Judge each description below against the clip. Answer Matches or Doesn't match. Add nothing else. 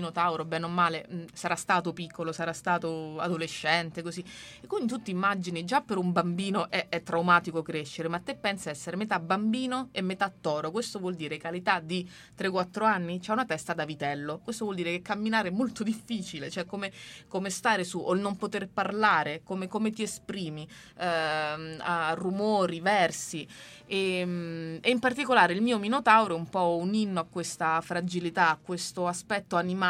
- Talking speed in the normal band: Doesn't match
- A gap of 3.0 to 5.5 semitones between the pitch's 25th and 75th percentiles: Matches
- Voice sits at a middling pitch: Matches